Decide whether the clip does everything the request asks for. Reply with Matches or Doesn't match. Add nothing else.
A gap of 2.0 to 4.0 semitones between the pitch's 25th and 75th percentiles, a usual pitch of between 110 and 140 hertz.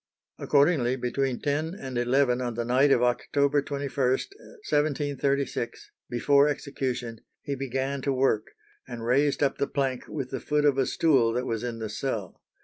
Matches